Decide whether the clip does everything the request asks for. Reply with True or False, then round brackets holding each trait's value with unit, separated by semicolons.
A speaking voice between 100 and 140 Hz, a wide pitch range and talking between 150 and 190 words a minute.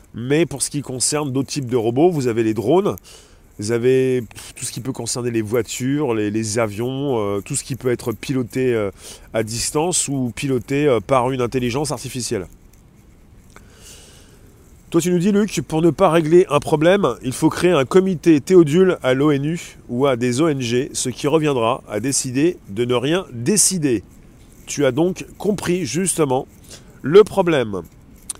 False (135 Hz; 4.7 semitones; 170 wpm)